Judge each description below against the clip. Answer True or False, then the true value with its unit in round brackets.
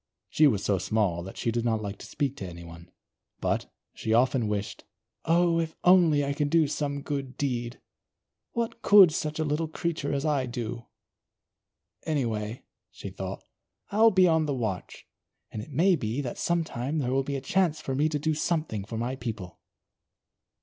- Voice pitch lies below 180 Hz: True (140 Hz)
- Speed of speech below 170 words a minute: False (185 wpm)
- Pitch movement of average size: False (5.7 semitones)